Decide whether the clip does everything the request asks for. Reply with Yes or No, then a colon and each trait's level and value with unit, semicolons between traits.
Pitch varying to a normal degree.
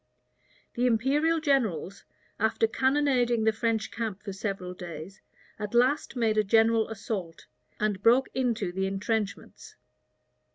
Yes: average, 3.6 semitones